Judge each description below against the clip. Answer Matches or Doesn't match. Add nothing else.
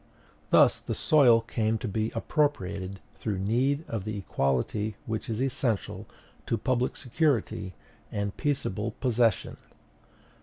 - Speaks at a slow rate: Matches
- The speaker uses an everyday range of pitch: Matches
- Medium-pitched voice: Doesn't match